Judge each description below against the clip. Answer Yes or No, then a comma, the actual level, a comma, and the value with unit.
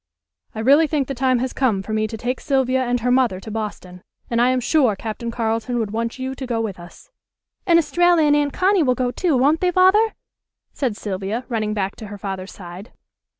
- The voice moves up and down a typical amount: Yes, average, 4.1 semitones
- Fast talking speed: Yes, fast, 220 wpm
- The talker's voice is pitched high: Yes, high, 245 Hz